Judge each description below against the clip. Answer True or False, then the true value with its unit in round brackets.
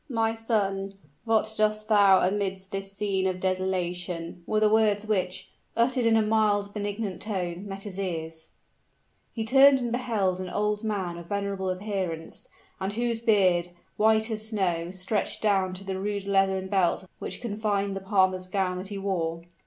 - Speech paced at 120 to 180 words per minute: True (165 wpm)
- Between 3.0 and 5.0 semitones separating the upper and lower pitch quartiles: False (2.4 semitones)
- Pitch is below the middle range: False (195 Hz)